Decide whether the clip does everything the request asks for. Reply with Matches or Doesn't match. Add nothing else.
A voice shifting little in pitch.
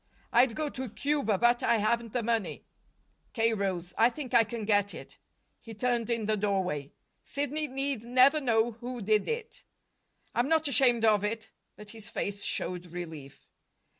Doesn't match